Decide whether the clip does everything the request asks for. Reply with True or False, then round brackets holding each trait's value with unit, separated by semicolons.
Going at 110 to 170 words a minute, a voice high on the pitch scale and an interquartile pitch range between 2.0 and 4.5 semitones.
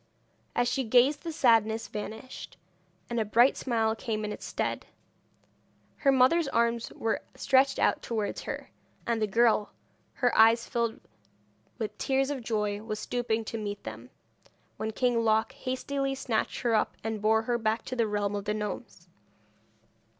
True (160 wpm; 225 Hz; 2.6 semitones)